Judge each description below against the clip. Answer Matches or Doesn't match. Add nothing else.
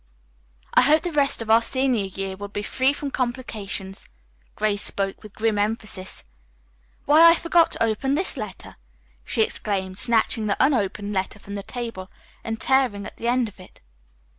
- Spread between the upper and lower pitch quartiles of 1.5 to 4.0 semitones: Doesn't match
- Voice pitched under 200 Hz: Doesn't match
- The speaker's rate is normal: Matches